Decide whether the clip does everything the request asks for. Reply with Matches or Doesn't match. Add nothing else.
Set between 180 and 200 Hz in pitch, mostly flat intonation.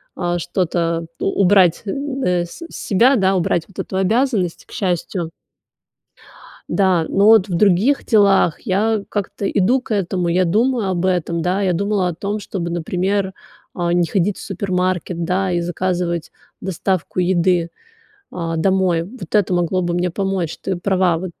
Matches